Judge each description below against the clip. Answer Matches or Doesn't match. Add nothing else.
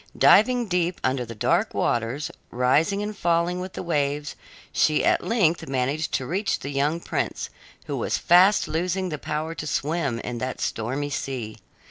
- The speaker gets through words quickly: Doesn't match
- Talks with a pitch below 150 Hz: Doesn't match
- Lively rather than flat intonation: Doesn't match